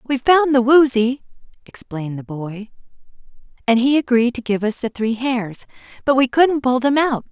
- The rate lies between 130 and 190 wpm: Yes, average, 180 wpm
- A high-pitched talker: Yes, high, 245 Hz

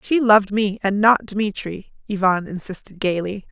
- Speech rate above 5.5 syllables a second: No, 4.7 syllables/s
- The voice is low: No, high, 205 Hz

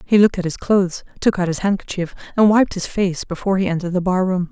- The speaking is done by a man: No, female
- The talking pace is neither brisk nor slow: No, fast, 240 wpm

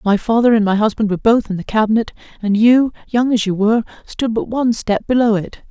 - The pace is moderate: No, fast, 230 wpm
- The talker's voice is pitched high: Yes, high, 220 Hz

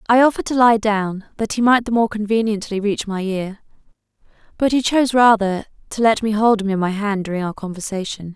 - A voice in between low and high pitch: No, high, 210 Hz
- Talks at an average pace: No, fast, 210 wpm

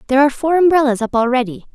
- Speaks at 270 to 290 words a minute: No, fast, 205 wpm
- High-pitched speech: Yes, very high, 265 Hz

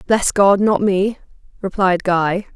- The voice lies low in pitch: No, high, 190 Hz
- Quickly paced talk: No, average, 140 wpm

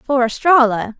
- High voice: Yes, very high, 250 Hz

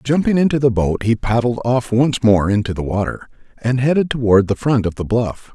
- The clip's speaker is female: No, male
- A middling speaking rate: No, fast, 215 wpm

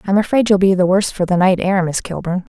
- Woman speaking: Yes, female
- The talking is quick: Yes, fast, 280 wpm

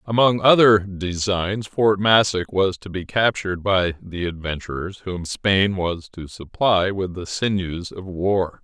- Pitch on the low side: Yes, very low, 95 Hz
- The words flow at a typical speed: Yes, average, 155 wpm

